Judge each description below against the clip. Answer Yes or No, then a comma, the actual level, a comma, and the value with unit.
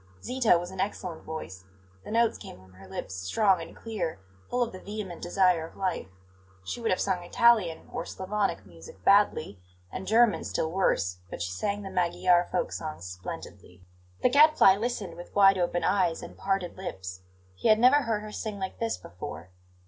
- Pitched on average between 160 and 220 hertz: Yes, medium, 185 Hz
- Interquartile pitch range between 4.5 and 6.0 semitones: Yes, average, 4.9 semitones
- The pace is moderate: Yes, average, 185 wpm